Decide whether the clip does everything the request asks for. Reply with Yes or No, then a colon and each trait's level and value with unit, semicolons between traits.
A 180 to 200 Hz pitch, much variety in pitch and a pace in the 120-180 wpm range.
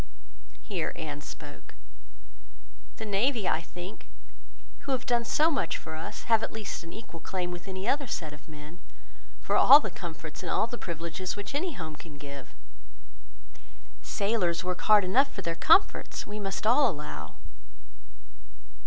Yes: medium, 185 Hz; wide, 5.7 semitones; average, 160 wpm